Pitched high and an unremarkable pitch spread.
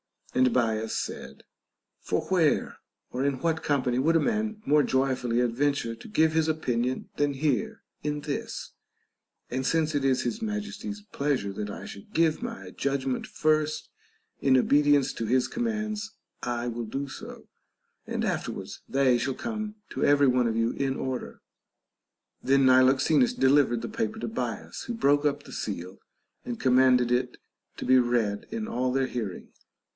No: low, 135 Hz; average, 4.3 semitones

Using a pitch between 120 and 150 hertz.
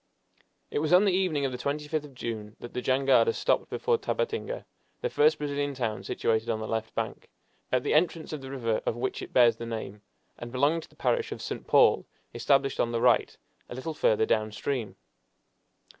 Yes: low, 135 Hz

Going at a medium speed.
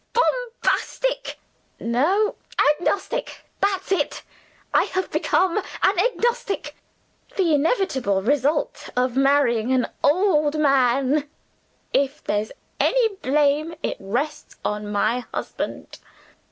No: slow, 100 wpm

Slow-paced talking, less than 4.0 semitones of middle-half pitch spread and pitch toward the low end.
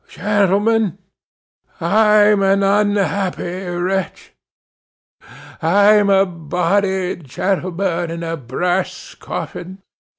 No: slow, 75 wpm; narrow, 2.5 semitones; high, 190 Hz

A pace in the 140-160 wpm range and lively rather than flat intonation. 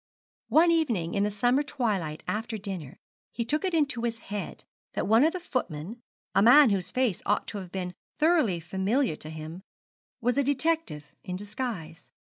No: average, 175 wpm; wide, 6.8 semitones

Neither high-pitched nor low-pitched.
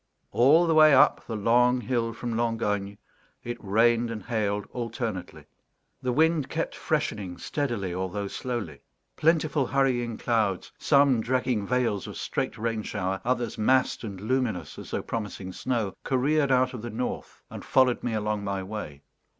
No: low, 115 Hz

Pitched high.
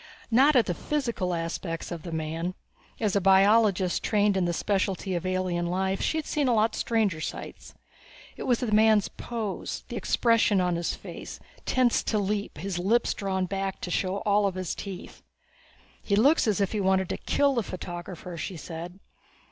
Yes: high, 195 Hz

